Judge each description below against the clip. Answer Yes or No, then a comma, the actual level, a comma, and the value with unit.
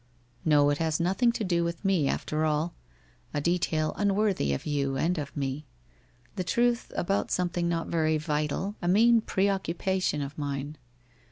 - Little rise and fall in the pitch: No, average, 4.3 semitones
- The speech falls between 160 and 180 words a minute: Yes, average, 170 wpm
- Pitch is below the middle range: No, medium, 165 Hz